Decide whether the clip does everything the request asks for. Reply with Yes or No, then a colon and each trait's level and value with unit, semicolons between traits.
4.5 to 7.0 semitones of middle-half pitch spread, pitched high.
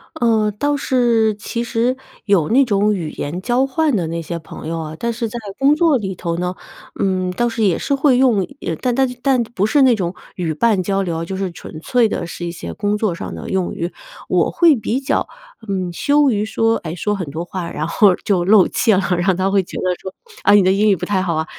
Yes: average, 5.1 semitones; high, 200 Hz